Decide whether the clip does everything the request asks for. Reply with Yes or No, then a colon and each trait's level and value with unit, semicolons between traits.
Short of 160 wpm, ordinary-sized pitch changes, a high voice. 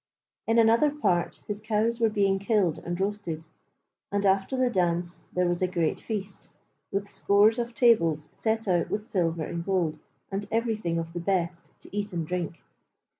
No: average, 175 wpm; average, 4.1 semitones; high, 195 Hz